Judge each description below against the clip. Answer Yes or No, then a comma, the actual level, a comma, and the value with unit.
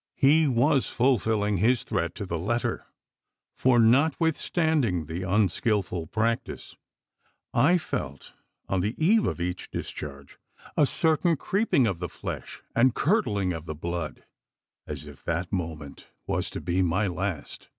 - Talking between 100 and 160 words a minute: Yes, average, 140 wpm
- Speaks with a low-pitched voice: Yes, low, 105 Hz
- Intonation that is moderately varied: No, wide, 7.6 semitones